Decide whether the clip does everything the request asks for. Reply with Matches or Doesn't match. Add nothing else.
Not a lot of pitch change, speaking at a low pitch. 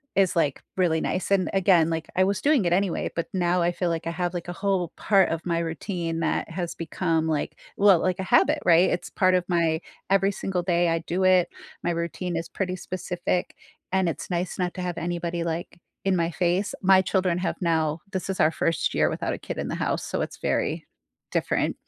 Doesn't match